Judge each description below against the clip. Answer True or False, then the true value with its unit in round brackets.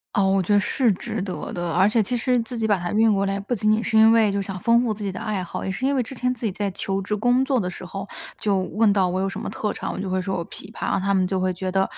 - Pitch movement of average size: True (3.0 semitones)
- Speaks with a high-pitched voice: True (200 Hz)